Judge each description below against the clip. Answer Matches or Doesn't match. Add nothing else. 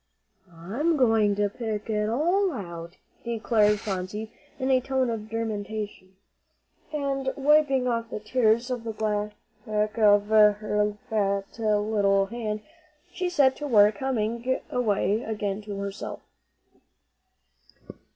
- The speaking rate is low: Matches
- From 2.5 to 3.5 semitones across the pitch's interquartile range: Matches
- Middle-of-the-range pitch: Doesn't match